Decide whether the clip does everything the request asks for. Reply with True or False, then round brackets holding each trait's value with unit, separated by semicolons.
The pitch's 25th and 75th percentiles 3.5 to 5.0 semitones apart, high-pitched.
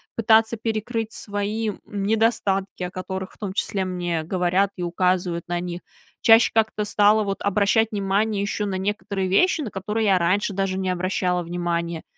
False (2.9 semitones; 195 Hz)